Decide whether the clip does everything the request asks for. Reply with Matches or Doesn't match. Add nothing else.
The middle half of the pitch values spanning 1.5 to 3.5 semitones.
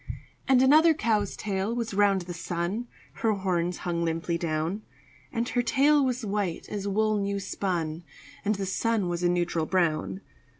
Doesn't match